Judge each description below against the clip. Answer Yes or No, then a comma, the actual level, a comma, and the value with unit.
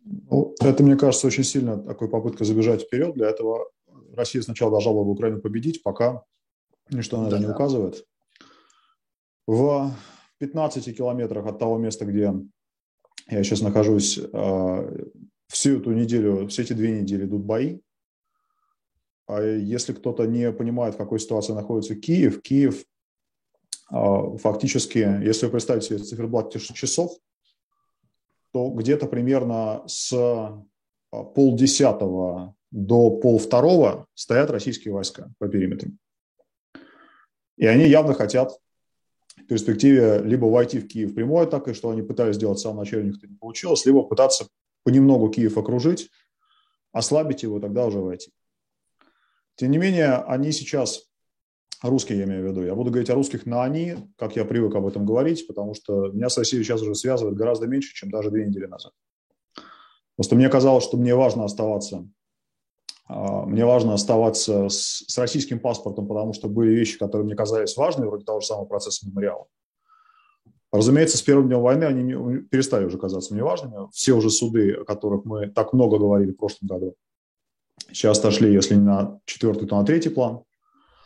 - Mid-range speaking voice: No, low, 115 Hz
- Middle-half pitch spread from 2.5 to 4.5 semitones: Yes, average, 4.2 semitones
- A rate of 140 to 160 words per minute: Yes, average, 155 wpm